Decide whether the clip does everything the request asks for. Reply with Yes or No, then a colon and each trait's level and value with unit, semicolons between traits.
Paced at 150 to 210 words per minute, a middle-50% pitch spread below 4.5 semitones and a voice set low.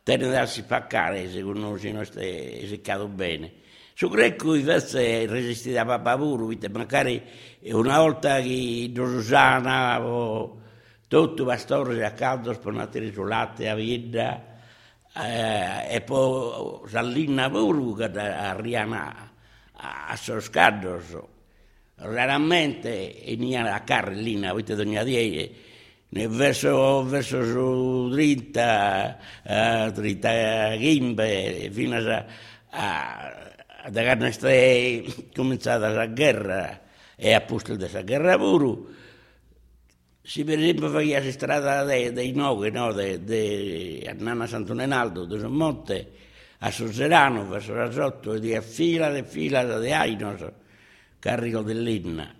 No: average, 135 wpm; average, 3.3 semitones; low, 115 Hz